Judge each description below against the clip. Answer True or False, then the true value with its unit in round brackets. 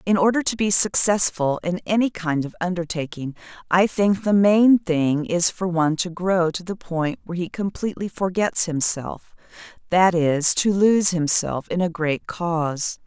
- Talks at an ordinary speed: True (170 wpm)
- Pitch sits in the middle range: True (180 Hz)